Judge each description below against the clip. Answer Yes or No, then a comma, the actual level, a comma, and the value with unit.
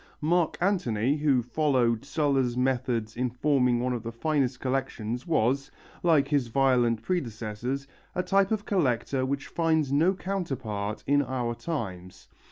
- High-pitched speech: No, low, 130 Hz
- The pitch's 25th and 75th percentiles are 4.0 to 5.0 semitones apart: Yes, average, 4.3 semitones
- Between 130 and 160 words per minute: Yes, average, 145 wpm